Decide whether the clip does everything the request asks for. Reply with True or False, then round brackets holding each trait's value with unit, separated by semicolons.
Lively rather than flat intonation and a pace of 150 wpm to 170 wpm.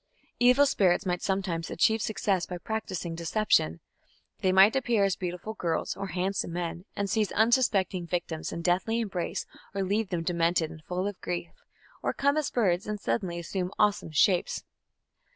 False (3.5 semitones; 165 wpm)